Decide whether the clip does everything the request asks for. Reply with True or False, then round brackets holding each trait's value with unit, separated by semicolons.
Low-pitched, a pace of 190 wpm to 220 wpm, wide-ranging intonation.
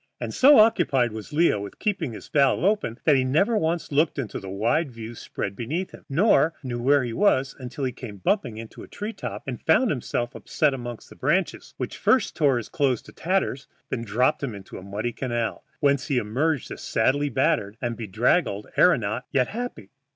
True (130 Hz; 200 wpm; 5.8 semitones)